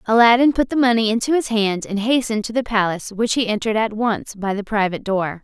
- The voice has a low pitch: No, high, 220 Hz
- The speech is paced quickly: Yes, fast, 230 wpm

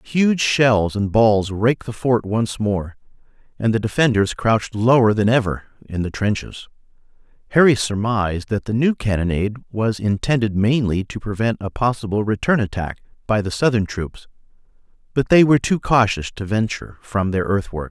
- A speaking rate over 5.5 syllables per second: No, 5.0 syllables/s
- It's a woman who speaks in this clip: No, male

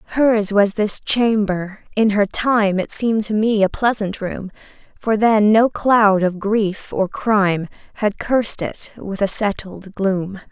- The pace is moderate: Yes, average, 165 wpm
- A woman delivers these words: Yes, female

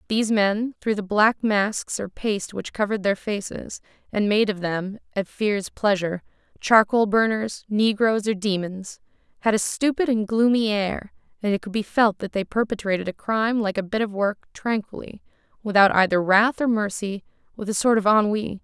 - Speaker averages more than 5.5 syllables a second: No, 5.0 syllables/s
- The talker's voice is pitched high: Yes, high, 210 Hz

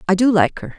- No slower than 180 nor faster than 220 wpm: No, fast, 305 wpm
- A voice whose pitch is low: No, high, 205 Hz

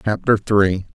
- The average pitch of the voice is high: No, low, 105 Hz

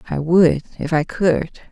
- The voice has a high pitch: No, medium, 165 Hz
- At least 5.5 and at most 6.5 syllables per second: No, 3.9 syllables/s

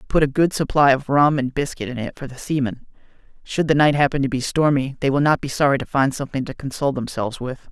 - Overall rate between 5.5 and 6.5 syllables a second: Yes, 6.4 syllables/s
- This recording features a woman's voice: No, male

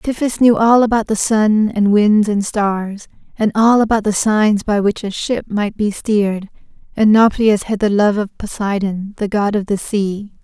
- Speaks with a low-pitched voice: No, high, 210 Hz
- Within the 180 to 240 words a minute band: Yes, average, 195 wpm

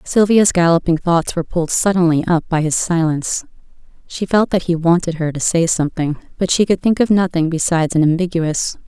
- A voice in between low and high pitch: Yes, medium, 170 Hz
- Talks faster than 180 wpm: Yes, average, 190 wpm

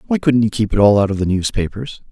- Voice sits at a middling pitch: No, low, 110 Hz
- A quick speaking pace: Yes, fast, 285 wpm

